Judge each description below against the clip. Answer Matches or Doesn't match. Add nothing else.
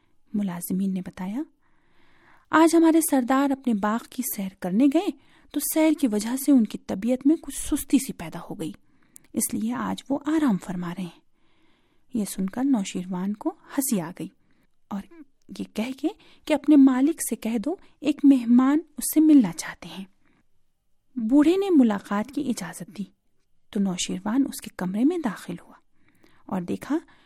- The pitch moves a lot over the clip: Matches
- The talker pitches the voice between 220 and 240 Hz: Doesn't match